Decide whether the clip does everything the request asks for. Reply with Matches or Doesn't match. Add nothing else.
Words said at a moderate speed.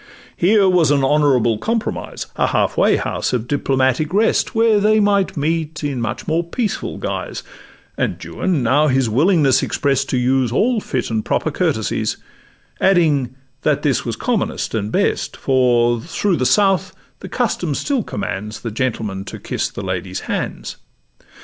Matches